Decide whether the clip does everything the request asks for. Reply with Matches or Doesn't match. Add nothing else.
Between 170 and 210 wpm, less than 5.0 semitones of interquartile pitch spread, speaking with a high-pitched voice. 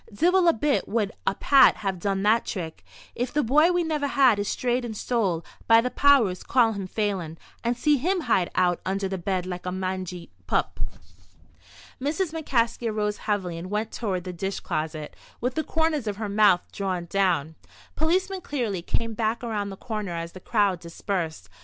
Doesn't match